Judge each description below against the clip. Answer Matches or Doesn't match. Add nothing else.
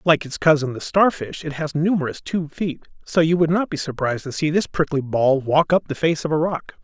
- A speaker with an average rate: Doesn't match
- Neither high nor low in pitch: Matches